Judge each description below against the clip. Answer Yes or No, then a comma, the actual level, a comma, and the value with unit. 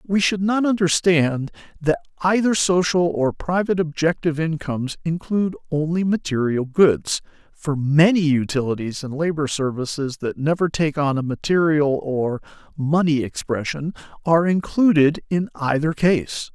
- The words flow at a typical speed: No, slow, 125 wpm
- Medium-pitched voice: Yes, medium, 160 Hz